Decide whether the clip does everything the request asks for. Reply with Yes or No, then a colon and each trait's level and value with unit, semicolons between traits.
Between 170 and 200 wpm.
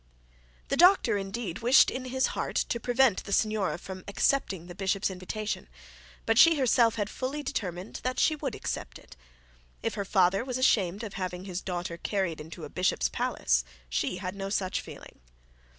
Yes: average, 175 wpm